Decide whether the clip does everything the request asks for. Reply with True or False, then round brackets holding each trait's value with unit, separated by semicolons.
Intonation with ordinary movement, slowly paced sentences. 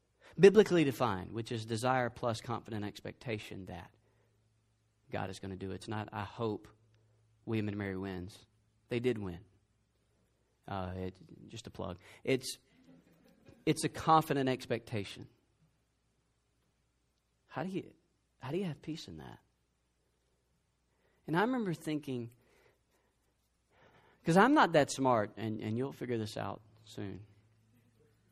True (3.7 semitones; 130 wpm)